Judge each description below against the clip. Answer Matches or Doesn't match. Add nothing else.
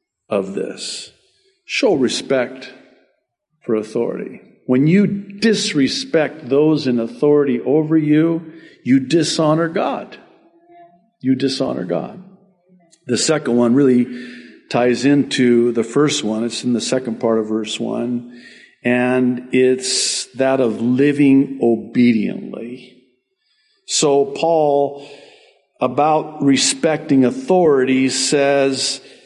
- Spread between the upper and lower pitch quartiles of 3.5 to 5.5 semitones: Matches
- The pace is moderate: Doesn't match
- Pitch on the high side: Doesn't match